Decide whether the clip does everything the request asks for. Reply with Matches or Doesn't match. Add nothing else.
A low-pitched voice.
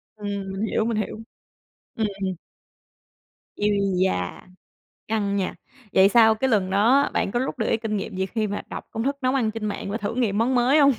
Doesn't match